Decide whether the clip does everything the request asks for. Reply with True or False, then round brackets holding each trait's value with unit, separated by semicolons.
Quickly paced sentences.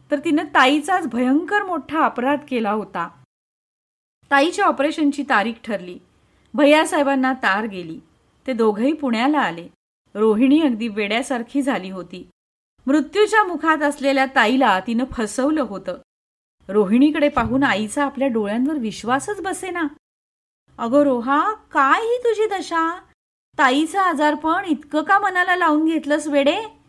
False (120 wpm)